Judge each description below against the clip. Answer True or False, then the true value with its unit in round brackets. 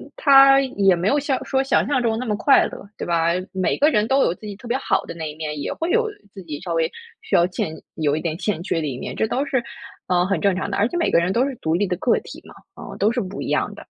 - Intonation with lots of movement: True (7.8 semitones)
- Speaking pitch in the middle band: False (205 Hz)